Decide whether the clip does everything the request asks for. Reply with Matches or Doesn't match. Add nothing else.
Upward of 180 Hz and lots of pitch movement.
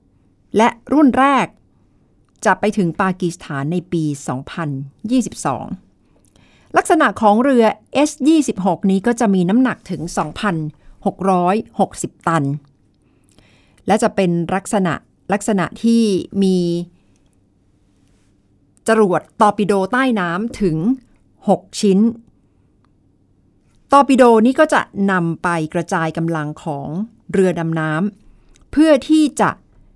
Matches